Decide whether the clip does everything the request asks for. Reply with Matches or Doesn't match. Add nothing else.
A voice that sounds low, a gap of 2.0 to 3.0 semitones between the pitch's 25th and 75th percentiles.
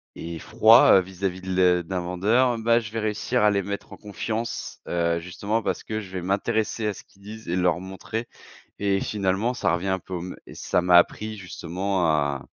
Doesn't match